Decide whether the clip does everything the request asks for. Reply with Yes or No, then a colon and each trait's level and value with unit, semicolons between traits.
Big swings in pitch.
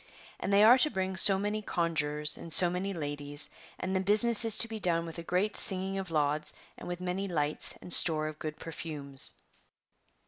No: average, 4.2 semitones